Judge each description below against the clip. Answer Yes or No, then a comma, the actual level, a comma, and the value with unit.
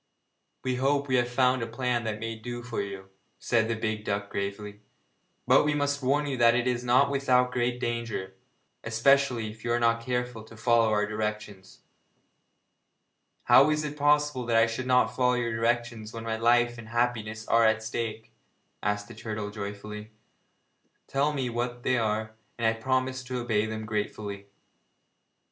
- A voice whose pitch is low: Yes, low, 115 Hz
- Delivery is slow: No, average, 175 wpm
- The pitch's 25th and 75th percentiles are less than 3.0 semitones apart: Yes, narrow, 2.4 semitones